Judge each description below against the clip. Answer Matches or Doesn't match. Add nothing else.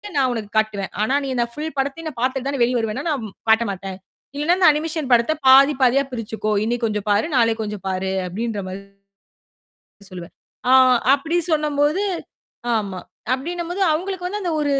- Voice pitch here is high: Matches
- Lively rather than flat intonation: Matches